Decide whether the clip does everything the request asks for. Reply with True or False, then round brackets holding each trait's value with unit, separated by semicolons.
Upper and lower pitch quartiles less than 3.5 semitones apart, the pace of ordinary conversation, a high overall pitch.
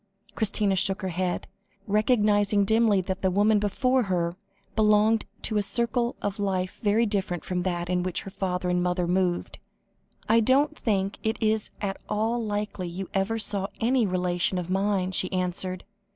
True (2.9 semitones; 170 wpm; 200 Hz)